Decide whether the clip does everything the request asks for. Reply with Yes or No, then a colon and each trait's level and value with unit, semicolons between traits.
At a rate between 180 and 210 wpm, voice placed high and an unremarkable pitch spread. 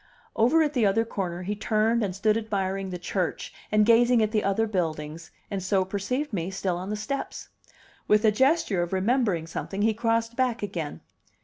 Yes: average, 190 wpm; high, 210 Hz; average, 3.4 semitones